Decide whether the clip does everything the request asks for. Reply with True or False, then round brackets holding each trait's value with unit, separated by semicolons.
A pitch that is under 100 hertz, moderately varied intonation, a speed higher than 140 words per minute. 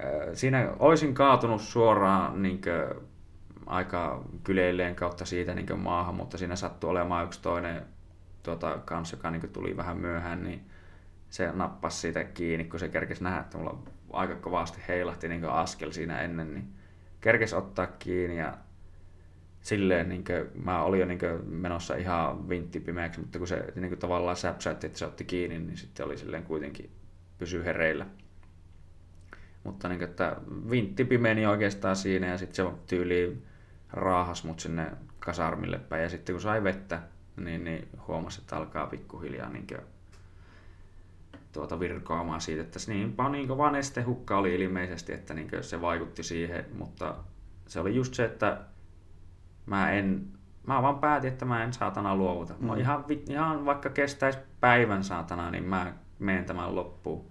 False (90 Hz; 2.2 semitones; 150 wpm)